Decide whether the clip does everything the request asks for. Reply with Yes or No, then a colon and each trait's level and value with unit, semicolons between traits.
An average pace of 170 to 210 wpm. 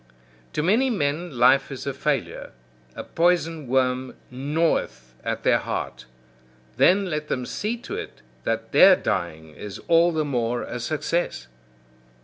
No: average, 140 wpm